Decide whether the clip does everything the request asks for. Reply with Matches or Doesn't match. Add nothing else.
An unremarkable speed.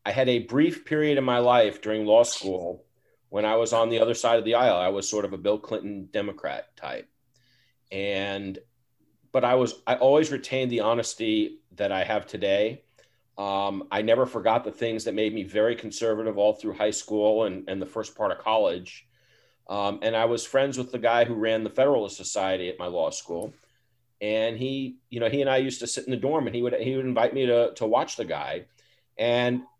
Doesn't match